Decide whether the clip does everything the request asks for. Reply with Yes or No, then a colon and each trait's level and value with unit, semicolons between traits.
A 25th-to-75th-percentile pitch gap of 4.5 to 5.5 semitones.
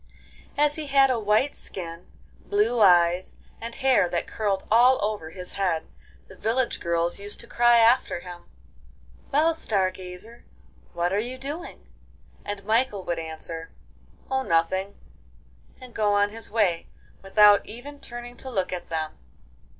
Yes: average, 5.2 semitones